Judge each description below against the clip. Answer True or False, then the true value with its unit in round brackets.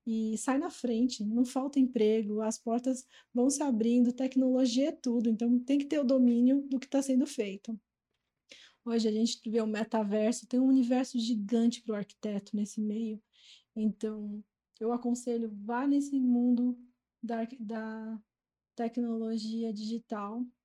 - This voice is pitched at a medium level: False (235 Hz)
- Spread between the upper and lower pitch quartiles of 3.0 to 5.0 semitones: False (2.5 semitones)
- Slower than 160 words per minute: True (150 wpm)